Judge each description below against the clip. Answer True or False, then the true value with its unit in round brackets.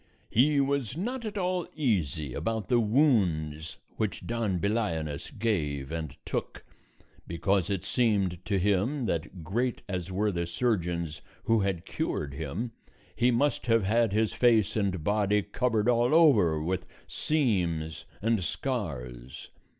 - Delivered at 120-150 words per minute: True (135 wpm)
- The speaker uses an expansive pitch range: True (5.9 semitones)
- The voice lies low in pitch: True (100 Hz)